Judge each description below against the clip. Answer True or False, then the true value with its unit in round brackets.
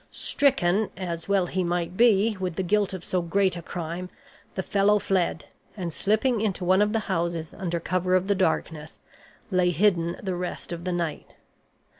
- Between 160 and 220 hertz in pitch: True (185 Hz)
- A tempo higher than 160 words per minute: True (180 wpm)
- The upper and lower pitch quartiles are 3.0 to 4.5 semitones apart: False (2.6 semitones)